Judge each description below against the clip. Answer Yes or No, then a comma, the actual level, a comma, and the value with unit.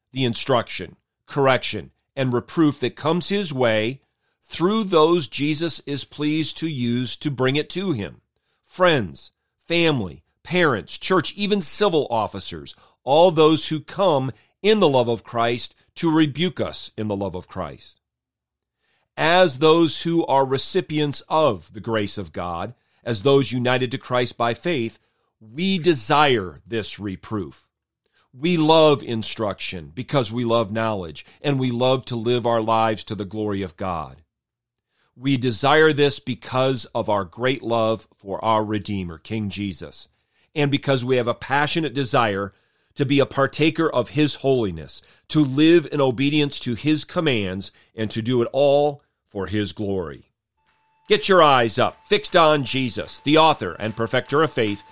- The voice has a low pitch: Yes, low, 130 Hz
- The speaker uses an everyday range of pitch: No, wide, 5.8 semitones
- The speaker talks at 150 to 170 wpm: Yes, average, 155 wpm